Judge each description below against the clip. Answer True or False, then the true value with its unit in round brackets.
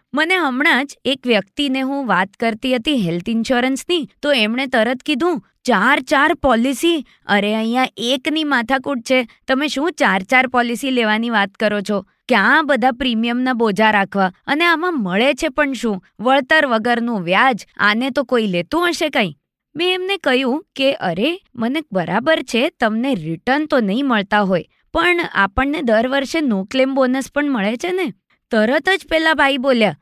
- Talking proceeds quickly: True (165 wpm)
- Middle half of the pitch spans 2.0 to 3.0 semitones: False (4.7 semitones)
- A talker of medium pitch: False (260 Hz)